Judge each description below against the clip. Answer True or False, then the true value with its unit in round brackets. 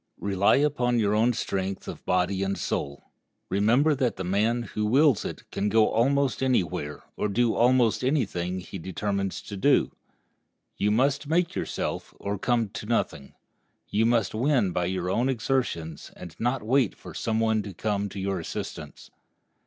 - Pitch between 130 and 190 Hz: False (110 Hz)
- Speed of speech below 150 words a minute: False (170 wpm)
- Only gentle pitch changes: False (4.2 semitones)